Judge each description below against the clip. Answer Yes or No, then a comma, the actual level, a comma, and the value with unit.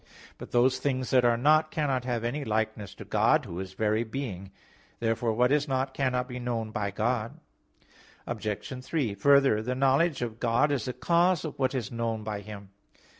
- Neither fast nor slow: Yes, average, 185 wpm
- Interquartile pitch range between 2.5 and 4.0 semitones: Yes, average, 3.7 semitones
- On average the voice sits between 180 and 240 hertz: No, low, 120 Hz